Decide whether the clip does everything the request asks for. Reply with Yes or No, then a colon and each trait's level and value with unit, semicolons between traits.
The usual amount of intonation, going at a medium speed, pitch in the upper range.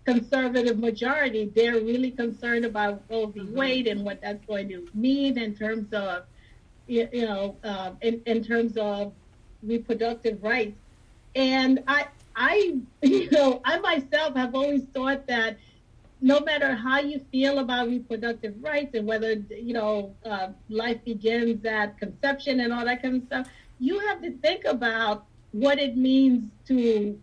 Yes: average, 3.7 semitones; average, 150 wpm; high, 235 Hz